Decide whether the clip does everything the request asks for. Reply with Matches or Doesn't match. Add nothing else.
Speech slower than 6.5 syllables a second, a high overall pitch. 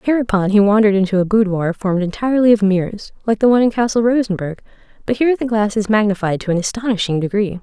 Doesn't match